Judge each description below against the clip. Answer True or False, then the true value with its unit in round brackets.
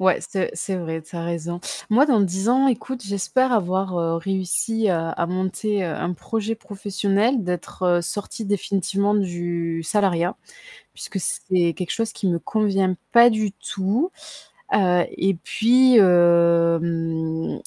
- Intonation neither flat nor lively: True (3.7 semitones)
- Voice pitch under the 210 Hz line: True (190 Hz)